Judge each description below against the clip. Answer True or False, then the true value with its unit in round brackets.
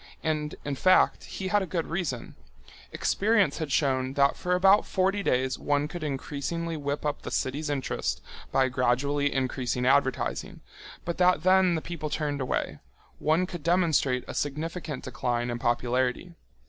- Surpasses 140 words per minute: True (150 wpm)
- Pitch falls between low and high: True (145 Hz)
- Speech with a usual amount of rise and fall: True (4.8 semitones)